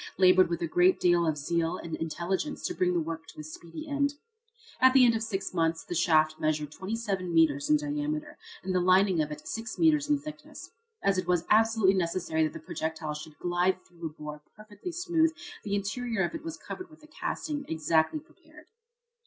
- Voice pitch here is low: No, medium, 185 Hz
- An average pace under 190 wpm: No, average, 200 wpm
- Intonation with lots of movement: Yes, wide, 7.1 semitones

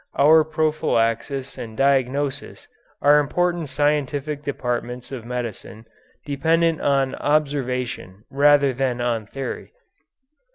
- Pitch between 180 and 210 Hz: No, medium, 140 Hz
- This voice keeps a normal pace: No, slow, 95 wpm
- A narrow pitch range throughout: No, average, 3.1 semitones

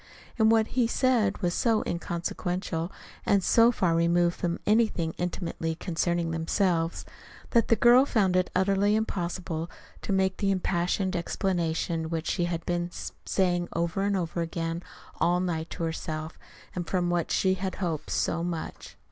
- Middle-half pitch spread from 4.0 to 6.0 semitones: No, narrow, 2.6 semitones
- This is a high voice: No, medium, 175 Hz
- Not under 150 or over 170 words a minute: Yes, average, 155 wpm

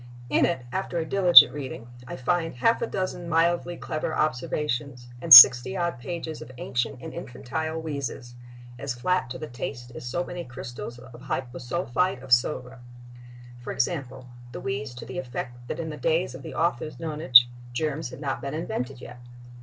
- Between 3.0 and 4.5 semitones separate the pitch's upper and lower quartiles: No, average, 5.0 semitones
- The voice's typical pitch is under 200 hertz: Yes, medium, 140 Hz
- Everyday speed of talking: Yes, average, 170 wpm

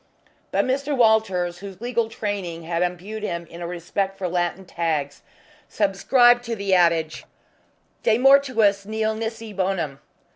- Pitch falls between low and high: No, high, 195 Hz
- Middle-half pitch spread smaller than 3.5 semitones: No, average, 4.2 semitones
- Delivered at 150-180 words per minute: No, average, 140 wpm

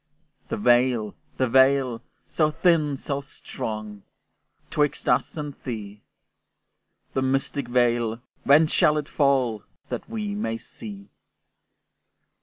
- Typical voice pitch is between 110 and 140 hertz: Yes, low, 135 Hz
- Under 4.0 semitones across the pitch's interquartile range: No, average, 4.3 semitones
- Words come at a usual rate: No, slow, 110 wpm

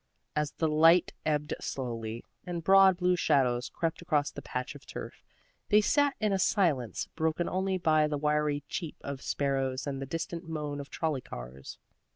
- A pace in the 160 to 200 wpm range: Yes, average, 175 wpm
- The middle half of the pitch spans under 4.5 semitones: Yes, average, 4.1 semitones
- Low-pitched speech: No, medium, 150 Hz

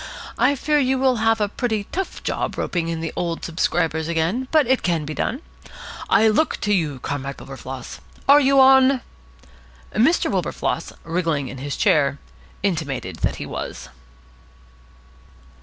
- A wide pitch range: Yes, wide, 8.9 semitones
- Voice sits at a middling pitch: Yes, medium, 180 Hz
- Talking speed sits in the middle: Yes, average, 150 wpm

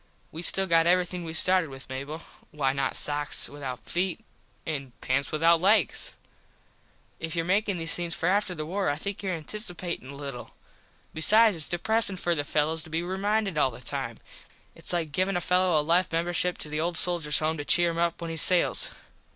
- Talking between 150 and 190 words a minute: No, average, 200 wpm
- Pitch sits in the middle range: Yes, medium, 165 Hz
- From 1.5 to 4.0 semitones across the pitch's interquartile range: Yes, average, 3.4 semitones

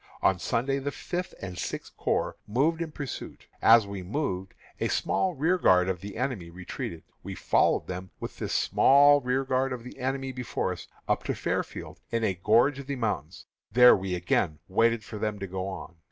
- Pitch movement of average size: No, wide, 6.2 semitones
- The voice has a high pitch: No, low, 115 Hz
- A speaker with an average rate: Yes, average, 185 wpm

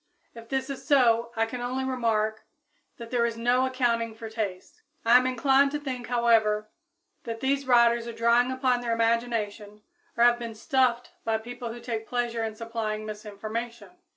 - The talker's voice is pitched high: Yes, high, 235 Hz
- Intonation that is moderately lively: No, narrow, 1.7 semitones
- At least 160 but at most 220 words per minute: Yes, average, 175 wpm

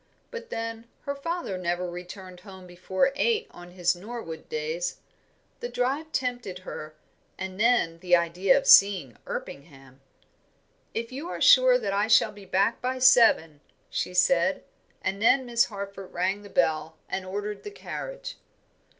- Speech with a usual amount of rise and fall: No, wide, 5.9 semitones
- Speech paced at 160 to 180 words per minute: No, average, 150 wpm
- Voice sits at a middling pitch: No, high, 195 Hz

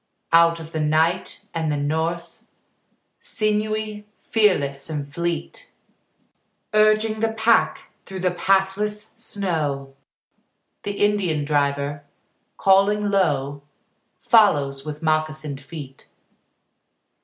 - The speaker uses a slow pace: Yes, slow, 95 wpm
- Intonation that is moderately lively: No, wide, 6.0 semitones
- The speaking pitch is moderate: Yes, medium, 170 Hz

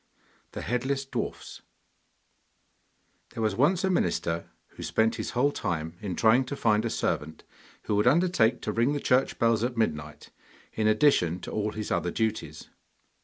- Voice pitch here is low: Yes, low, 110 Hz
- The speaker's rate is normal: Yes, average, 165 wpm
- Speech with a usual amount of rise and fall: Yes, average, 4.2 semitones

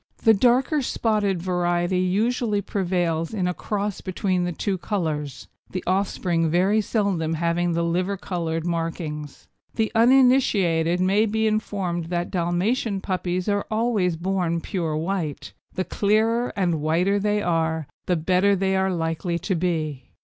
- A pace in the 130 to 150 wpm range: Yes, average, 140 wpm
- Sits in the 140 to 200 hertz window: Yes, medium, 185 Hz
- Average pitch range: Yes, average, 3.4 semitones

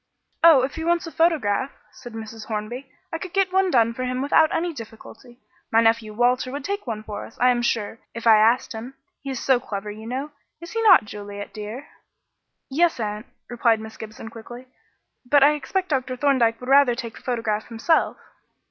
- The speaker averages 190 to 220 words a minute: Yes, average, 200 wpm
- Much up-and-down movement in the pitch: No, average, 4.2 semitones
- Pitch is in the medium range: No, high, 245 Hz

